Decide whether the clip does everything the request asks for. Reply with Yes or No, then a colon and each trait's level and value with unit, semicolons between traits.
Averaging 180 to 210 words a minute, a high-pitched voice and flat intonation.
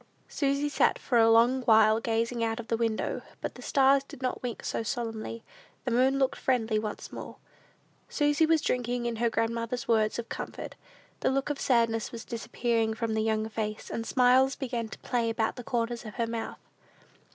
Yes: average, 190 wpm; high, 235 Hz; narrow, 2.1 semitones